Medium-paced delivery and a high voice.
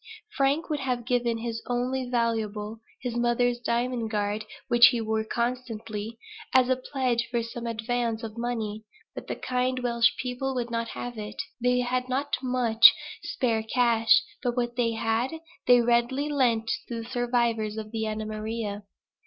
Yes: average, 160 wpm; high, 235 Hz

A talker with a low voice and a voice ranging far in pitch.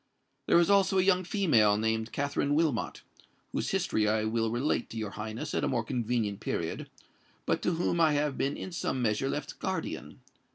Yes: low, 125 Hz; wide, 6.8 semitones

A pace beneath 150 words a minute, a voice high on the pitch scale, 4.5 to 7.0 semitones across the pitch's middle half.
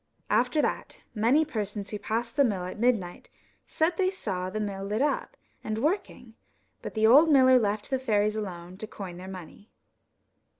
No: average, 175 wpm; high, 215 Hz; average, 4.8 semitones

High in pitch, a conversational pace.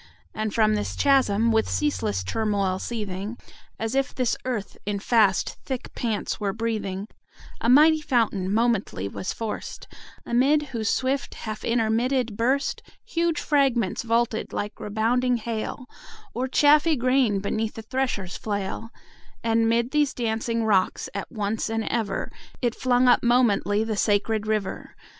Yes: high, 225 Hz; average, 145 wpm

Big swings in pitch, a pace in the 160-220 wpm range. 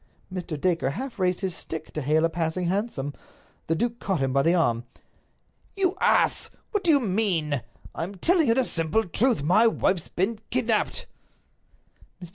Yes: wide, 6.1 semitones; average, 175 wpm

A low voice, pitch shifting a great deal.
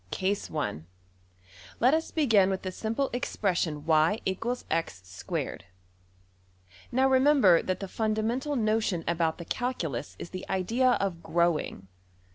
No: high, 190 Hz; wide, 6.6 semitones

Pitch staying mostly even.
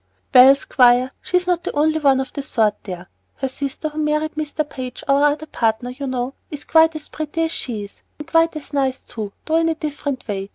No: average, 3.6 semitones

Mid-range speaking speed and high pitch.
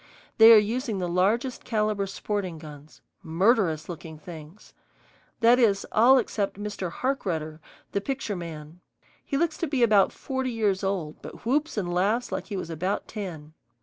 Yes: average, 160 wpm; high, 200 Hz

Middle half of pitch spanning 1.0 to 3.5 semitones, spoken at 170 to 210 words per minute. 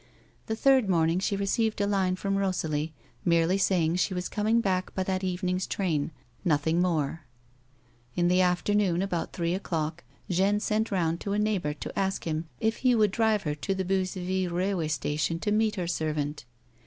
Yes: average, 3.2 semitones; average, 185 wpm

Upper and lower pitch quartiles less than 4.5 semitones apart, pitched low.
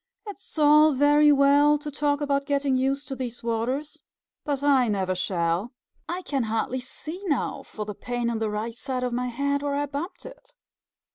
No: average, 3.7 semitones; very high, 275 Hz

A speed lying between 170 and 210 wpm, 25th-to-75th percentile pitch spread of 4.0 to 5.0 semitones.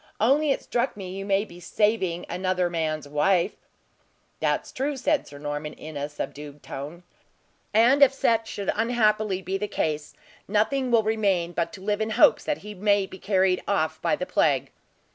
Yes: average, 180 wpm; average, 4.6 semitones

